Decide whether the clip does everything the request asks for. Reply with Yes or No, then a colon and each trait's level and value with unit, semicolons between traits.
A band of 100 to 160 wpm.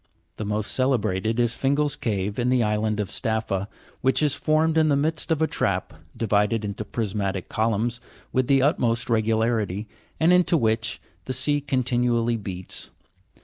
Yes: average, 155 wpm